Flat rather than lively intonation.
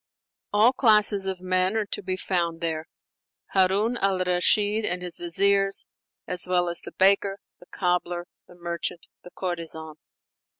Yes: narrow, 2.2 semitones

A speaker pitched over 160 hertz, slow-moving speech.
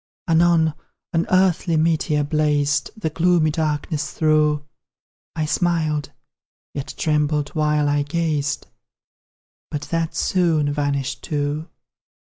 No: medium, 155 Hz; slow, 100 wpm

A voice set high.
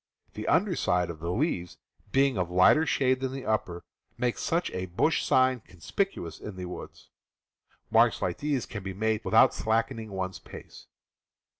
No: low, 110 Hz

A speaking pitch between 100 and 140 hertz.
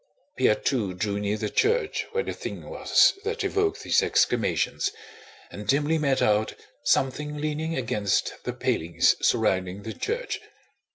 Yes: low, 135 Hz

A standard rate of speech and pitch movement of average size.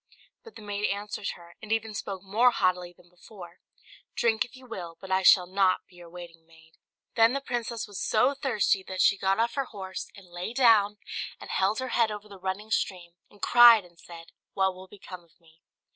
No: fast, 210 wpm; average, 3.8 semitones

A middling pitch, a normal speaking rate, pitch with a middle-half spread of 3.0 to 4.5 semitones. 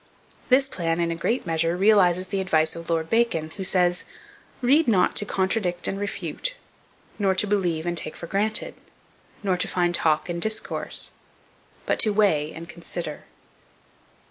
Yes: medium, 180 Hz; average, 160 wpm; average, 3.5 semitones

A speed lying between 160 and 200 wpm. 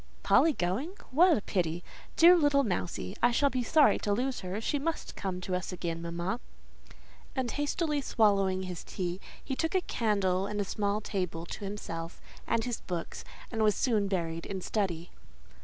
Yes: average, 175 wpm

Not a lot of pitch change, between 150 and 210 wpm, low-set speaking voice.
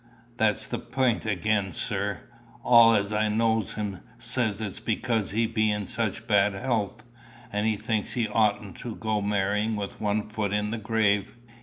Yes: narrow, 1.6 semitones; average, 165 wpm; low, 110 Hz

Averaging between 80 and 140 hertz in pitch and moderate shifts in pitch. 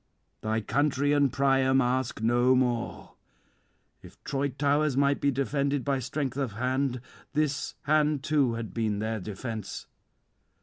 Yes: low, 135 Hz; average, 3.0 semitones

